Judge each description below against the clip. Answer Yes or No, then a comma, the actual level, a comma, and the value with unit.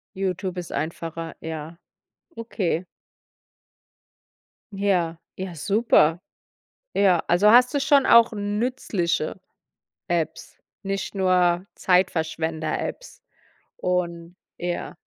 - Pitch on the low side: No, medium, 180 Hz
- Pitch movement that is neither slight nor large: Yes, average, 3.3 semitones